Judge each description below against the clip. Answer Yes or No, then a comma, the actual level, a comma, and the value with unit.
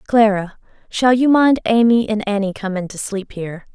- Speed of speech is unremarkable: Yes, average, 160 wpm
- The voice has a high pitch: Yes, high, 215 Hz